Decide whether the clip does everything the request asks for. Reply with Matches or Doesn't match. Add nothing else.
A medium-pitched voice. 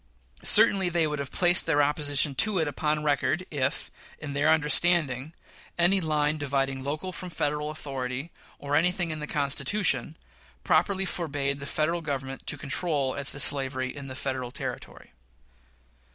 Matches